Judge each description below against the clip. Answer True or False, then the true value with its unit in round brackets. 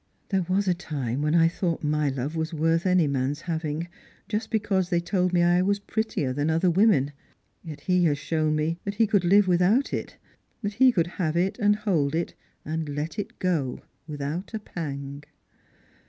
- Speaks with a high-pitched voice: False (170 Hz)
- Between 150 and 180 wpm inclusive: False (195 wpm)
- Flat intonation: False (4.0 semitones)